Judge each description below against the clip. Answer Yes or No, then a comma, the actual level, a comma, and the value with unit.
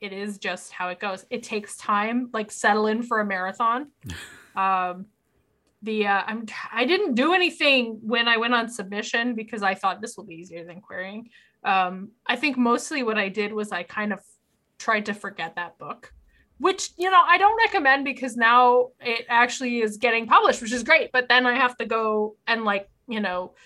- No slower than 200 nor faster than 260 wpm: Yes, fast, 205 wpm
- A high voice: Yes, high, 225 Hz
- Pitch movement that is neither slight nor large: Yes, average, 3.6 semitones